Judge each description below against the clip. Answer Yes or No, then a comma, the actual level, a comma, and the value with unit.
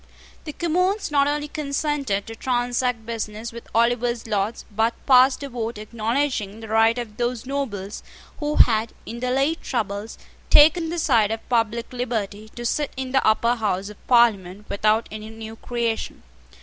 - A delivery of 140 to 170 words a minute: Yes, average, 160 wpm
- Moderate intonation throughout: Yes, average, 3.4 semitones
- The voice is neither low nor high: No, high, 235 Hz